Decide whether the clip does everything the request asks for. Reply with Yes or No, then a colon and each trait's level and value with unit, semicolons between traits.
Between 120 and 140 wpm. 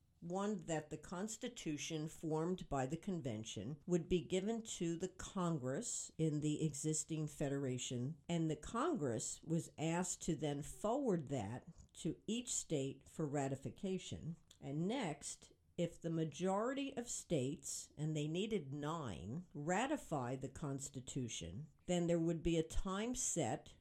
Yes: slow, 135 wpm